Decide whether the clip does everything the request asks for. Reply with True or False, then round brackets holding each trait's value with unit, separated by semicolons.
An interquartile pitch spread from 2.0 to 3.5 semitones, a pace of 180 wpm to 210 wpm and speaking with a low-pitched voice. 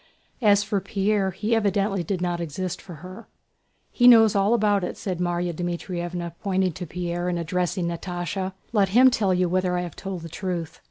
False (2.4 semitones; 185 wpm; 185 Hz)